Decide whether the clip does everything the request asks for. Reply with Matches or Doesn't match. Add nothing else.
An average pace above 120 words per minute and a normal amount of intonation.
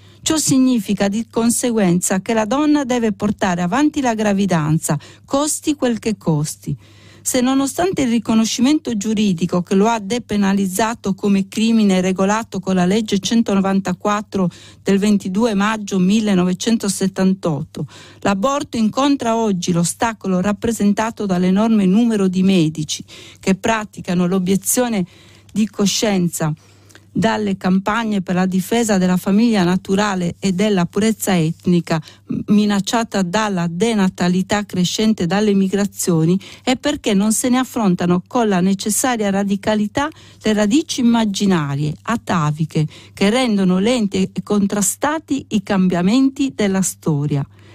Doesn't match